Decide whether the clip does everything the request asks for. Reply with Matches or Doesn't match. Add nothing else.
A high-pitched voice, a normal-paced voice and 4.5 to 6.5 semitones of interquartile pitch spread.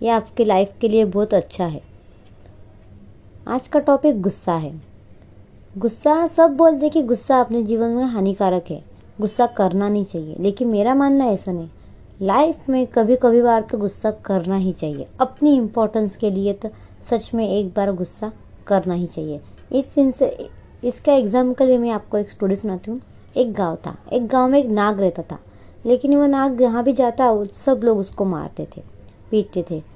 Matches